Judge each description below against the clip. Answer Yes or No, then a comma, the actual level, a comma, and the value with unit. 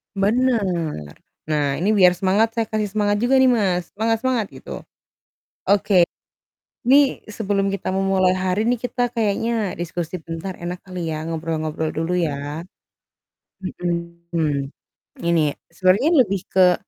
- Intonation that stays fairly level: No, average, 4.0 semitones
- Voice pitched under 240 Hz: Yes, medium, 185 Hz